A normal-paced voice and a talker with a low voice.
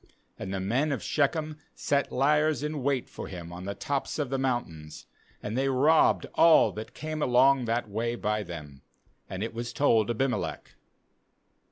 Yes: average, 170 wpm; low, 125 Hz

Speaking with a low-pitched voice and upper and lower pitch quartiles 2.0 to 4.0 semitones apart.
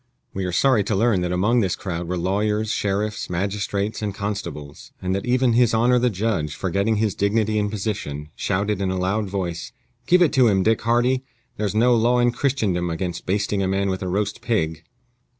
Yes: low, 100 Hz; average, 3.3 semitones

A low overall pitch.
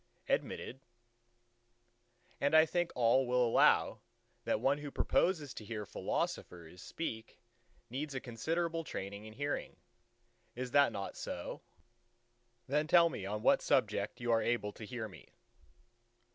Yes: low, 125 Hz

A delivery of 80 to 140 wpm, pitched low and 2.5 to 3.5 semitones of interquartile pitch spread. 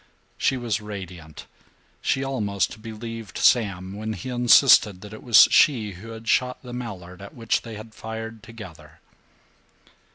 No: average, 150 wpm; low, 110 Hz; average, 2.9 semitones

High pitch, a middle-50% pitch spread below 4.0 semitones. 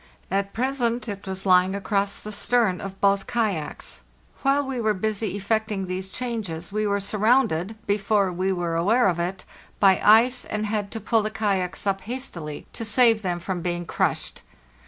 Yes: high, 200 Hz; average, 3.0 semitones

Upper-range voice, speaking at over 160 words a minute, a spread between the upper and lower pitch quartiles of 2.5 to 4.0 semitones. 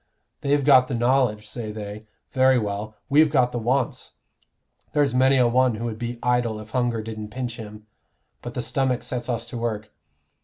No: low, 120 Hz; average, 180 wpm; average, 3.0 semitones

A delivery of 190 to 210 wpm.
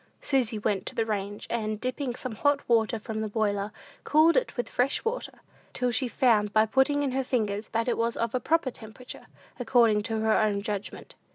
Yes: average, 200 wpm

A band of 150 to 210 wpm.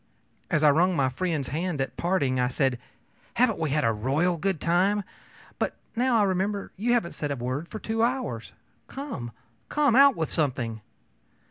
Yes: average, 175 wpm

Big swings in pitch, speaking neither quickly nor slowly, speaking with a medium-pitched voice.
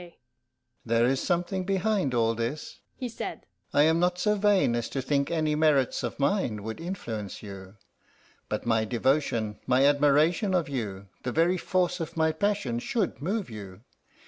Yes: wide, 7.4 semitones; average, 165 wpm; medium, 145 Hz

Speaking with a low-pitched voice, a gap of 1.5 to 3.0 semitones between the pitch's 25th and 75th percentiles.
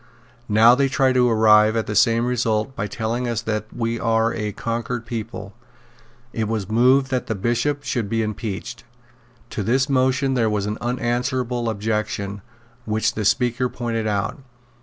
Yes: low, 115 Hz; narrow, 2.5 semitones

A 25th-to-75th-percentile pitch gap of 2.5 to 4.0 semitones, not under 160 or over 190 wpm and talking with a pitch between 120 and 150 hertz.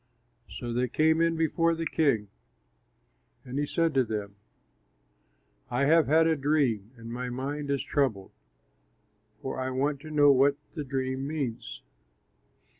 No: average, 3.7 semitones; average, 145 wpm; medium, 140 Hz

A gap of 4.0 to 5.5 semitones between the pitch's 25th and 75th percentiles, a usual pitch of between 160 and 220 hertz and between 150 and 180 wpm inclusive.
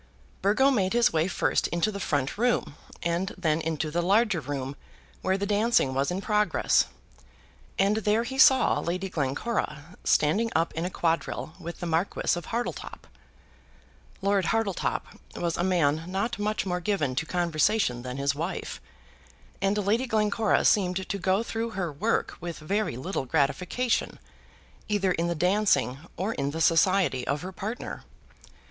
Yes: average, 4.6 semitones; medium, 185 Hz; average, 155 wpm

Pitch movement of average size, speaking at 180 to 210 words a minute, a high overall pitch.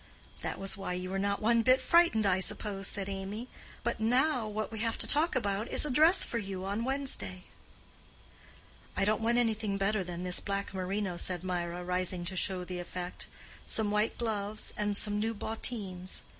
Yes: average, 3.4 semitones; average, 185 wpm; high, 205 Hz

